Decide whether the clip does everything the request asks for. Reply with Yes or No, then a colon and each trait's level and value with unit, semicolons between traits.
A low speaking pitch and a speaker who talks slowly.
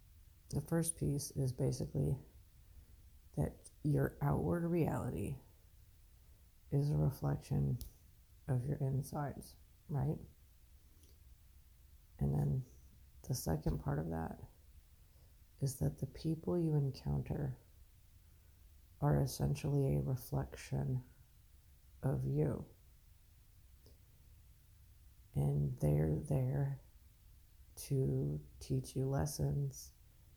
Yes: very low, 90 Hz; slow, 85 wpm